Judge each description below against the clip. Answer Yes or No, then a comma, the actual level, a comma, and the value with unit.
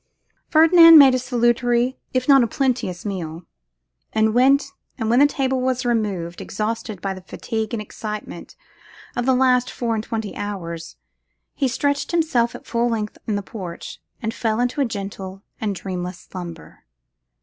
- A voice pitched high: Yes, high, 230 Hz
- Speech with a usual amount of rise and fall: Yes, average, 4.4 semitones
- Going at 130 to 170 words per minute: Yes, average, 155 wpm